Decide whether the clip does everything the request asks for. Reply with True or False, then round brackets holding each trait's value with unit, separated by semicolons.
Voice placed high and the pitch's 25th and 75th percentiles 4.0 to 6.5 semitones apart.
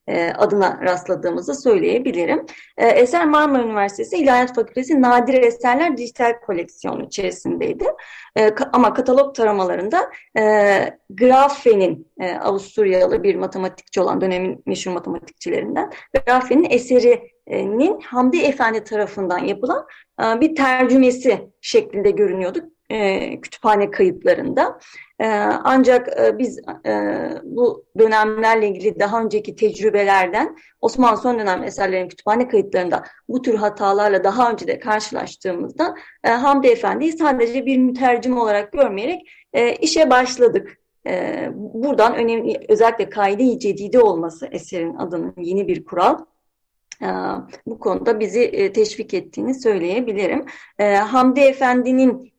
True (235 Hz; 5.0 semitones)